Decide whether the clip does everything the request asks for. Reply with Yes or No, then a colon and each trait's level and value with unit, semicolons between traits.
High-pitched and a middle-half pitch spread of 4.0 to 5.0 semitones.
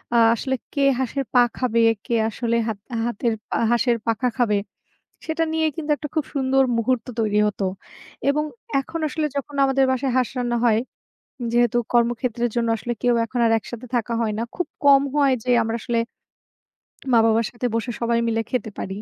No: high, 240 Hz; average, 2.7 semitones